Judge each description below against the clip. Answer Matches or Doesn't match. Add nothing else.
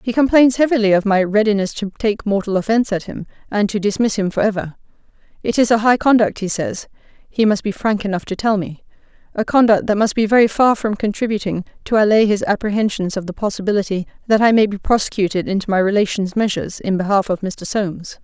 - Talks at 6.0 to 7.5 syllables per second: Matches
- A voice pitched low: Doesn't match